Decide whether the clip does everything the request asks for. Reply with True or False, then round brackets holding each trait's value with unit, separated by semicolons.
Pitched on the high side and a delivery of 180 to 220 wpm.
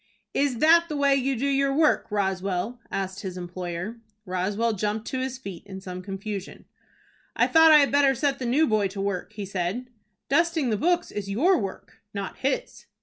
True (220 Hz; 190 wpm)